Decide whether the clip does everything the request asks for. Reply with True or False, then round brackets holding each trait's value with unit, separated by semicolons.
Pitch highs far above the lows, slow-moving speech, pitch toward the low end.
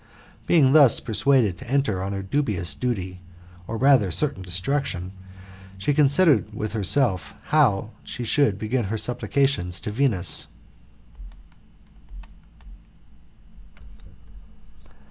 True (6.5 semitones; 100 wpm; 110 Hz)